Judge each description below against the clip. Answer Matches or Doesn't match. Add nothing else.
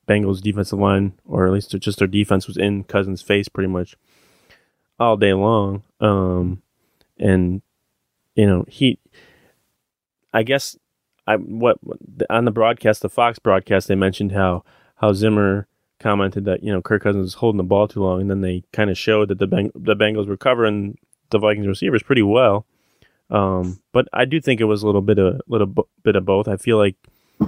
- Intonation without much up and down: Matches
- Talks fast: Doesn't match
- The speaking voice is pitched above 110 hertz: Doesn't match